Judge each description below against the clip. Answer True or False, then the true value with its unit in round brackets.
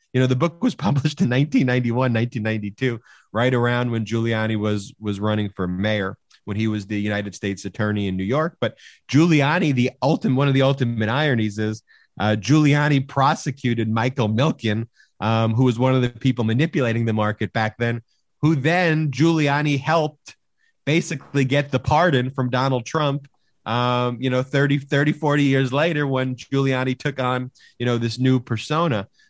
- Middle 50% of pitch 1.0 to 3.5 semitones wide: False (4.3 semitones)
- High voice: False (130 Hz)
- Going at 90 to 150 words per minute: False (170 wpm)